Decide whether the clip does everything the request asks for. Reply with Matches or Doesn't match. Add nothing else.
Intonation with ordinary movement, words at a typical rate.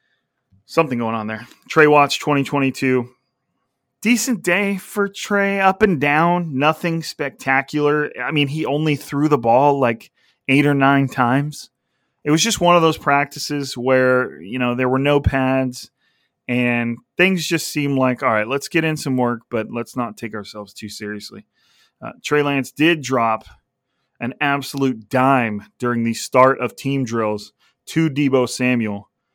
Matches